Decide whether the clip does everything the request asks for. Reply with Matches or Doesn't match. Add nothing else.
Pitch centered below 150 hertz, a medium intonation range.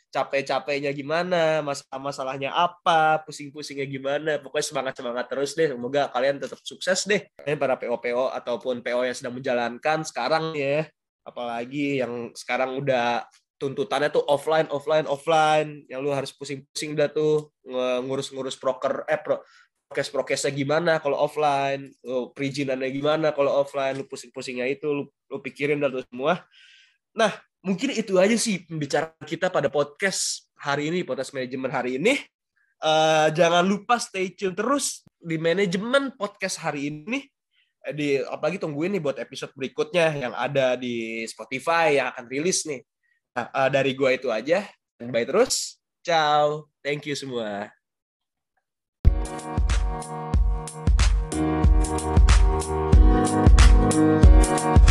Matches